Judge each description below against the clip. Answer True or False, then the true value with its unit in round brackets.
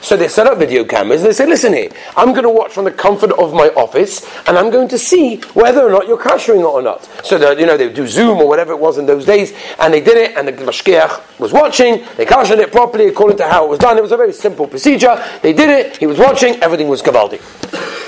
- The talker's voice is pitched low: False (240 Hz)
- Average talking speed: False (270 wpm)